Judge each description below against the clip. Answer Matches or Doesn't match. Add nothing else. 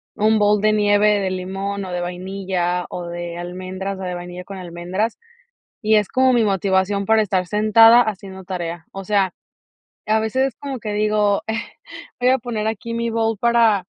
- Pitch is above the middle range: Matches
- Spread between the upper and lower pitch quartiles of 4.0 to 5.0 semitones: Doesn't match